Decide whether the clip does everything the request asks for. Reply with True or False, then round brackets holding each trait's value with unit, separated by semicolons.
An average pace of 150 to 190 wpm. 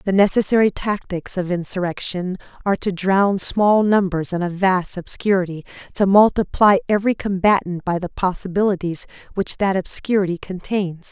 False (135 wpm)